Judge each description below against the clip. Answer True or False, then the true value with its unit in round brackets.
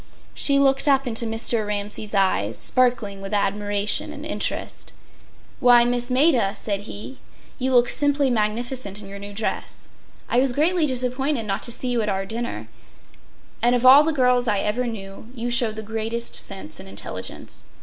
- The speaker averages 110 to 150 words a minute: False (170 wpm)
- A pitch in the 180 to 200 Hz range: False (235 Hz)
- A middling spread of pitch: True (3.6 semitones)